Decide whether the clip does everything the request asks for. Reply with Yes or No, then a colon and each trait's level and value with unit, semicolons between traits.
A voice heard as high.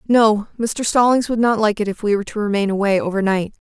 Yes: high, 215 Hz